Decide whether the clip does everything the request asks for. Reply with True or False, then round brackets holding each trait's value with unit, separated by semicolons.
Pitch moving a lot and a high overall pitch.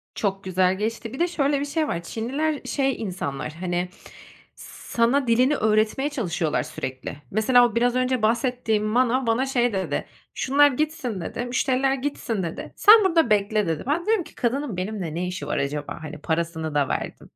True (6.5 semitones; 230 Hz)